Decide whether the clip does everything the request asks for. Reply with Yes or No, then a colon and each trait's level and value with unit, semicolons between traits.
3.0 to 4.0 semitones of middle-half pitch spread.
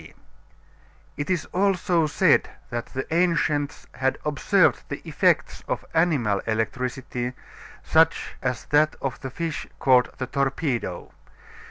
No: average, 4.4 semitones